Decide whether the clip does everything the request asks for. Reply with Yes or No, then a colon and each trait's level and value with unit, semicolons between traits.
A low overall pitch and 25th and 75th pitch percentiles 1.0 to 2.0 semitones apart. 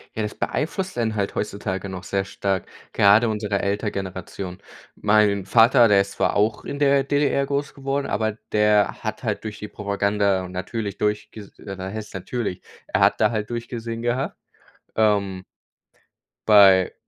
No: low, 105 Hz; average, 2.7 semitones